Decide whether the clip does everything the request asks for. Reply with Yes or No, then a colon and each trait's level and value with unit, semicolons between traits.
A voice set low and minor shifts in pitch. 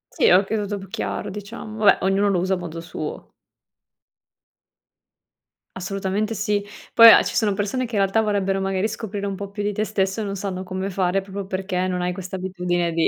No: high, 195 Hz; narrow, 1.6 semitones